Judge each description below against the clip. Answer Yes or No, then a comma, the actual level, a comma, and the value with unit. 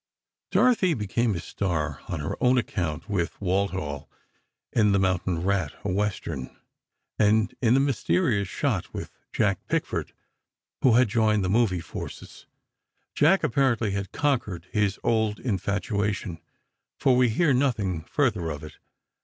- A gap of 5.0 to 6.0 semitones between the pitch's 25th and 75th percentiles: No, average, 4.6 semitones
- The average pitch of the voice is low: Yes, low, 100 Hz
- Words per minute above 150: No, slow, 135 wpm